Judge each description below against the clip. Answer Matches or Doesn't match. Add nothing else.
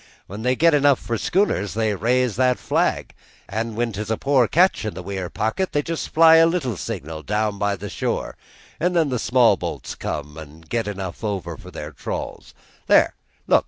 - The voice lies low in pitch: Matches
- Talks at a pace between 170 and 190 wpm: Doesn't match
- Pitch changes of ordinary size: Doesn't match